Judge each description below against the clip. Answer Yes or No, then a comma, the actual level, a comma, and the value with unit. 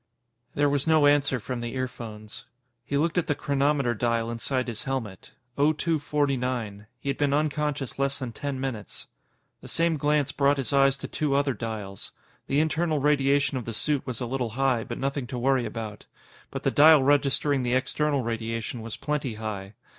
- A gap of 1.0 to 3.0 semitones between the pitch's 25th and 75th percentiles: No, average, 3.5 semitones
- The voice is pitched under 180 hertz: Yes, low, 135 Hz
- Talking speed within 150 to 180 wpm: No, average, 190 wpm